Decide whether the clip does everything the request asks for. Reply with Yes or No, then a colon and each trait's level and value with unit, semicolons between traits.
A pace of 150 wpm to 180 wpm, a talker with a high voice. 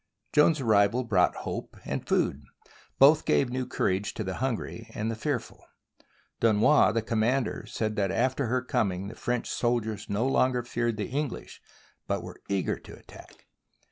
No: average, 165 wpm; low, 115 Hz